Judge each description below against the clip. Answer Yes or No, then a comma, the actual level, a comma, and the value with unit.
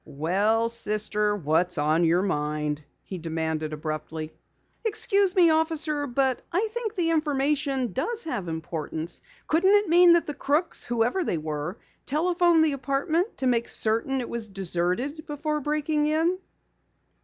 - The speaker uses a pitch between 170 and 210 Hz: No, very high, 260 Hz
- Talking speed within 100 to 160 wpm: Yes, average, 145 wpm